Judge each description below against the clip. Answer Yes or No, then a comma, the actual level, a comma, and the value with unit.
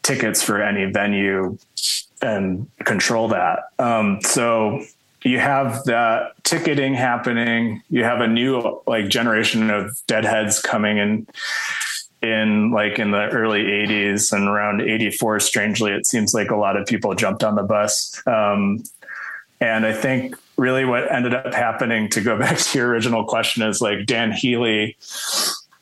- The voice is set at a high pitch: No, low, 110 Hz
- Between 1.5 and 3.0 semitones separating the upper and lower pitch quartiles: Yes, narrow, 2.5 semitones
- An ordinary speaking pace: Yes, average, 150 wpm